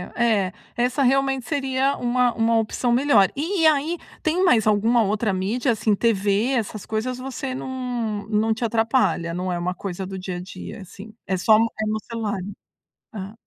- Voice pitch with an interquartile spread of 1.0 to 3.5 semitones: No, average, 4.0 semitones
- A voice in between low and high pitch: No, high, 225 Hz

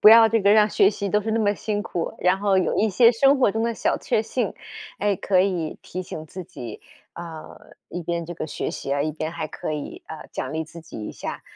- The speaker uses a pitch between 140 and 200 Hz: Yes, high, 190 Hz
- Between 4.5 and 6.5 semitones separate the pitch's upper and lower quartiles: Yes, average, 5.0 semitones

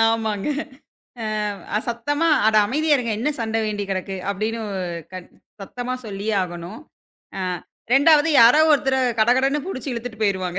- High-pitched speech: Yes, high, 225 Hz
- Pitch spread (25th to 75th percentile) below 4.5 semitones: No, average, 4.9 semitones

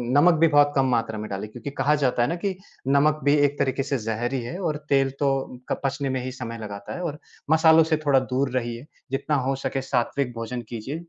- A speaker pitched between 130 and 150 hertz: Yes, low, 135 Hz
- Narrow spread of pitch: No, average, 3.0 semitones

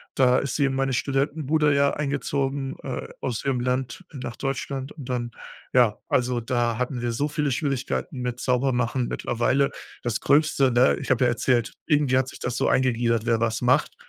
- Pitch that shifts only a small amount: Yes, narrow, 2.2 semitones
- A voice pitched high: No, low, 130 Hz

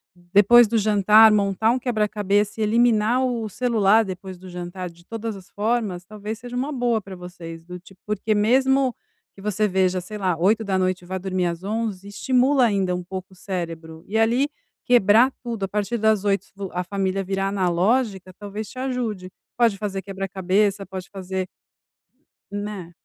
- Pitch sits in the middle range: No, high, 200 Hz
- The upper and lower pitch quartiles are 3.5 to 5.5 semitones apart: No, average, 3.1 semitones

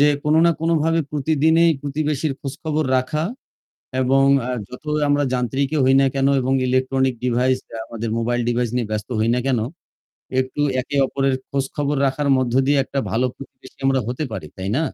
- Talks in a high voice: No, low, 135 Hz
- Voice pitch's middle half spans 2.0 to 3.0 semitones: Yes, average, 2.7 semitones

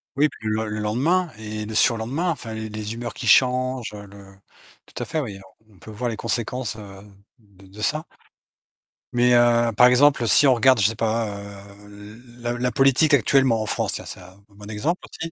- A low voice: Yes, low, 115 Hz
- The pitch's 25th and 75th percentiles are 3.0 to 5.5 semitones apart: Yes, average, 3.3 semitones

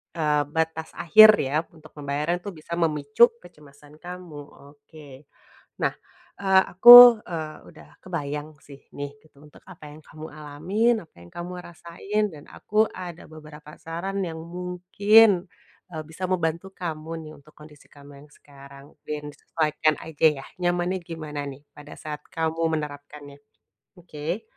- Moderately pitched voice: Yes, medium, 160 Hz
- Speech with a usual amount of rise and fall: Yes, average, 3.2 semitones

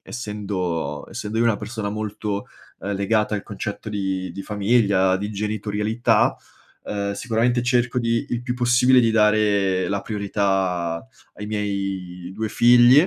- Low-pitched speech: Yes, low, 105 Hz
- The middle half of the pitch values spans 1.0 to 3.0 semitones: Yes, average, 2.7 semitones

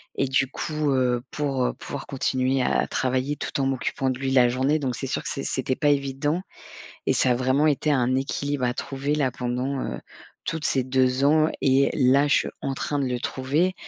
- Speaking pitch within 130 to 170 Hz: Yes, low, 135 Hz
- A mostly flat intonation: Yes, narrow, 1.8 semitones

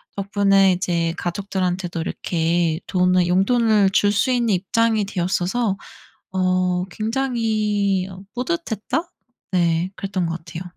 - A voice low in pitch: No, high, 190 Hz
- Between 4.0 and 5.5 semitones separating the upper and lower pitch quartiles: No, average, 3.2 semitones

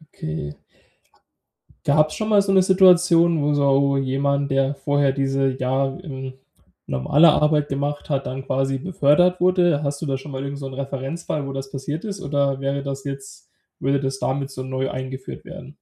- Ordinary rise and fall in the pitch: No, narrow, 2.1 semitones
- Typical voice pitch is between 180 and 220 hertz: No, medium, 140 Hz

